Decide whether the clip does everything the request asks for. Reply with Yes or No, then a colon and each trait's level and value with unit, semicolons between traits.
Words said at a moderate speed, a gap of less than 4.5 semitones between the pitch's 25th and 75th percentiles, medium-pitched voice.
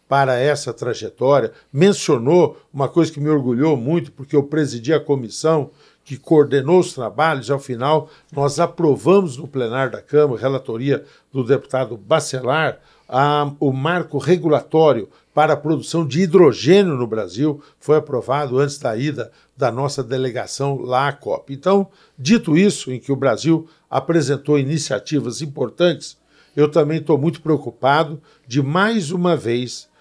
Yes: average, 145 wpm; average, 2.8 semitones; medium, 145 Hz